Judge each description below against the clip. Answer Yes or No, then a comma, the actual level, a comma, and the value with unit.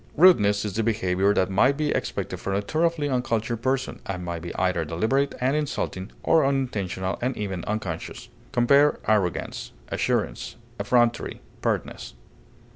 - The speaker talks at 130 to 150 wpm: Yes, average, 140 wpm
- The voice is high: No, low, 110 Hz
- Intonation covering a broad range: Yes, wide, 6.2 semitones